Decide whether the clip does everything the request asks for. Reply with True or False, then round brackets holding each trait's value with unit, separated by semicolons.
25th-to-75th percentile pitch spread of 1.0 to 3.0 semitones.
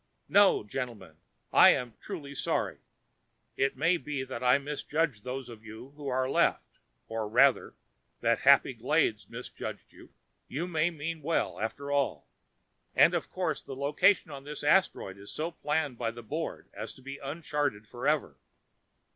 False (3.7 semitones)